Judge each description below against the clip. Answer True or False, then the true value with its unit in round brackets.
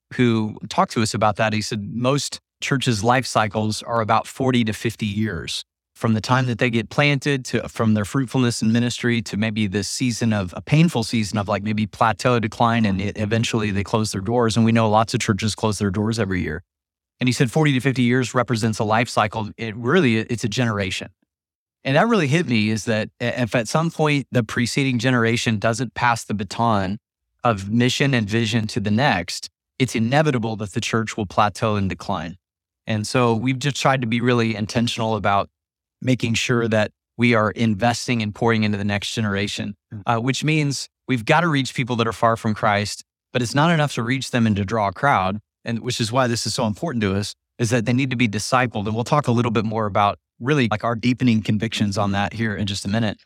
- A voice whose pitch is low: True (115 Hz)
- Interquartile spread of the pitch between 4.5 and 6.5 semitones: False (2.5 semitones)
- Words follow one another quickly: True (220 wpm)